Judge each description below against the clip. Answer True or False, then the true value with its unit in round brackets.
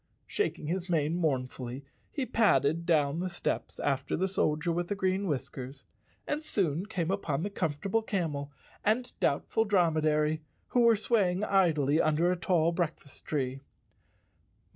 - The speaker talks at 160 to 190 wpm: True (165 wpm)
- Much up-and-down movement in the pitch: False (4.5 semitones)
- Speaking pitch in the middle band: True (170 Hz)